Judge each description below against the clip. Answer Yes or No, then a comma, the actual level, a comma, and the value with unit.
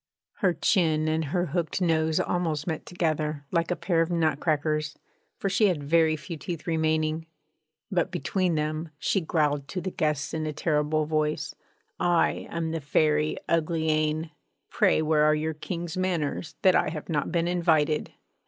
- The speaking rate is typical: Yes, average, 165 wpm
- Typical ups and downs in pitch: No, narrow, 1.8 semitones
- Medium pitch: Yes, medium, 160 Hz